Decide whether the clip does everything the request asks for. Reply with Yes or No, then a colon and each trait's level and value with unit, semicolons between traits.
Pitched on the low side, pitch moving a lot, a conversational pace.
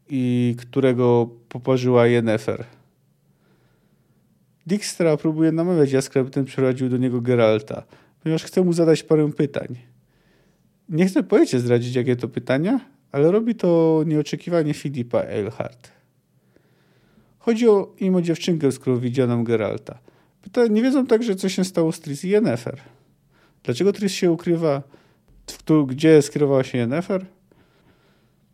No: medium, 150 Hz; wide, 6.2 semitones; average, 120 wpm